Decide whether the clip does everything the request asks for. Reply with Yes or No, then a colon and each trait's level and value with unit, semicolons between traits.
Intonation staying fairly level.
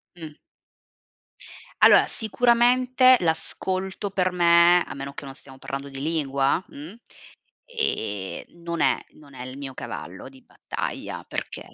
No: wide, 5.7 semitones